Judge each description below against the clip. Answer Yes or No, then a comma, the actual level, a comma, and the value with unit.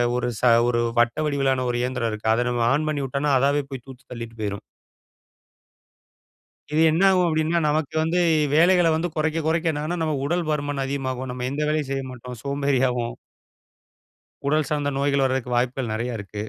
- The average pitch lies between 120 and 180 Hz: Yes, low, 135 Hz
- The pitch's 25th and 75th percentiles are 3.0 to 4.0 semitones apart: Yes, average, 3.6 semitones